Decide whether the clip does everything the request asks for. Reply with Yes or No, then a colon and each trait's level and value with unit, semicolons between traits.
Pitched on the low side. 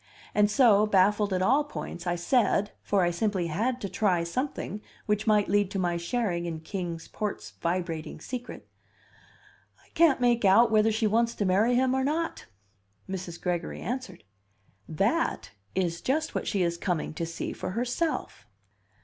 No: high, 205 Hz